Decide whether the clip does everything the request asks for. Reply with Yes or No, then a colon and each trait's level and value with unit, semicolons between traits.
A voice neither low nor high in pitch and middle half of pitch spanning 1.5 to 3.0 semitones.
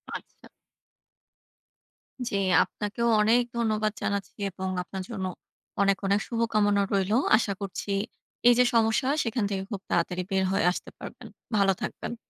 No: high, 205 Hz; narrow, 2.5 semitones